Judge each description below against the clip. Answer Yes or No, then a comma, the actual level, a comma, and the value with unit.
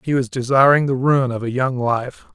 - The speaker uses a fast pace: Yes, fast, 230 wpm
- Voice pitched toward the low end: Yes, low, 130 Hz